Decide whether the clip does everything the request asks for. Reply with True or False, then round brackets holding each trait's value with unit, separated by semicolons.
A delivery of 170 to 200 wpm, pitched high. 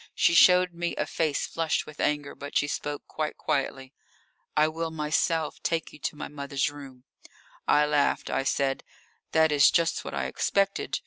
False (175 wpm; 150 Hz)